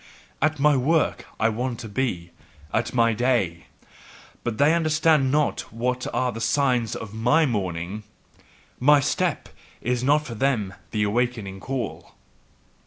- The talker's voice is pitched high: No, low, 125 Hz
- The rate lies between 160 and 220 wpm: No, average, 140 wpm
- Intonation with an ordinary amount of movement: Yes, average, 4.2 semitones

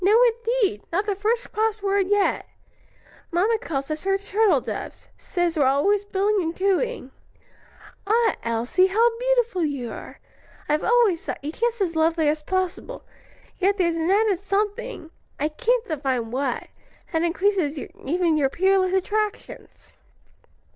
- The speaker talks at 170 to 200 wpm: No, average, 145 wpm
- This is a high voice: Yes, very high, 380 Hz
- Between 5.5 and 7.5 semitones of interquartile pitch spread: No, average, 5.1 semitones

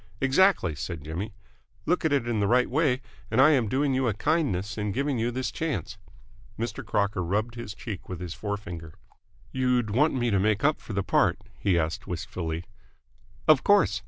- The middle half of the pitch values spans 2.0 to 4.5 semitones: No, wide, 5.5 semitones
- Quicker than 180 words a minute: Yes, average, 190 wpm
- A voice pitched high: No, low, 110 Hz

